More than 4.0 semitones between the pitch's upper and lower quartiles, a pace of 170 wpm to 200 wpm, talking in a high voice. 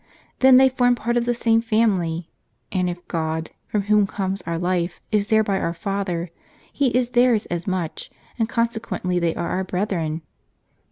Yes: average, 4.8 semitones; average, 175 wpm; high, 195 Hz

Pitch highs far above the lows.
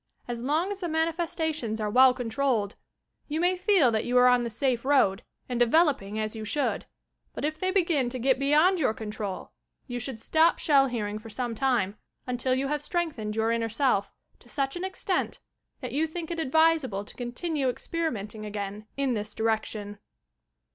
Yes: wide, 6.2 semitones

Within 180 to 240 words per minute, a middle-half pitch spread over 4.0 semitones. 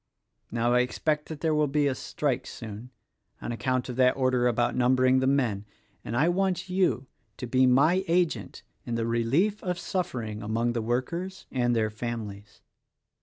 Yes: average, 185 wpm; average, 4.5 semitones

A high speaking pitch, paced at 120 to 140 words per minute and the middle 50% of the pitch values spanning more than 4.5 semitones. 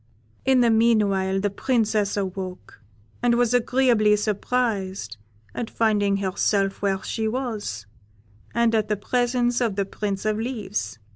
No: high, 215 Hz; slow, 135 wpm; average, 3.3 semitones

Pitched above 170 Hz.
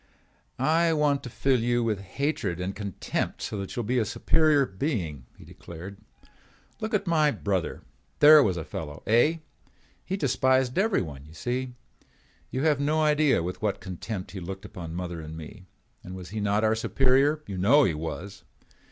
No: low, 110 Hz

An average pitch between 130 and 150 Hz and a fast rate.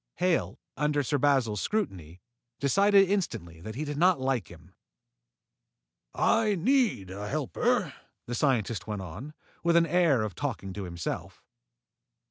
No: medium, 140 Hz; slow, 135 wpm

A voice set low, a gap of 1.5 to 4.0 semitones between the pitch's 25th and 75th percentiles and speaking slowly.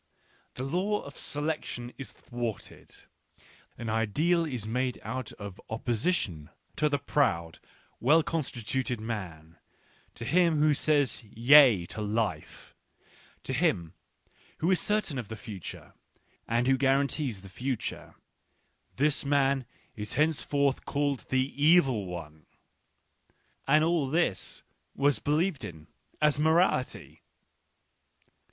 No: low, 130 Hz; wide, 5.5 semitones; slow, 120 wpm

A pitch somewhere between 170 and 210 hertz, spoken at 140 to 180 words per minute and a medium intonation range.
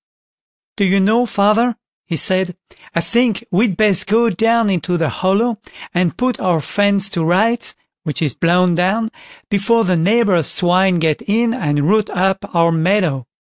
Yes: high, 190 Hz; average, 160 wpm; average, 4.2 semitones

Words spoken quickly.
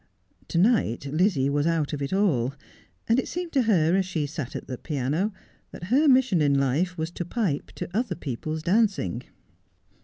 No: average, 185 wpm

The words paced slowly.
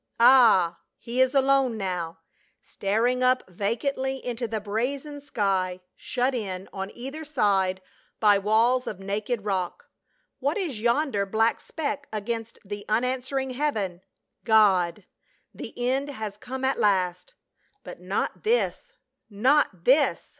Yes: slow, 130 wpm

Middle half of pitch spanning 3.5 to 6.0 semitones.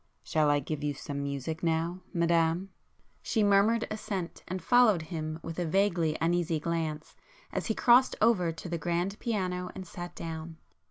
No: average, 3.1 semitones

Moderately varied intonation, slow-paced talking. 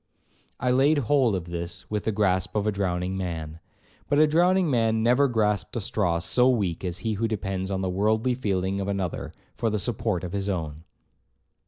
No: average, 4.1 semitones; average, 195 wpm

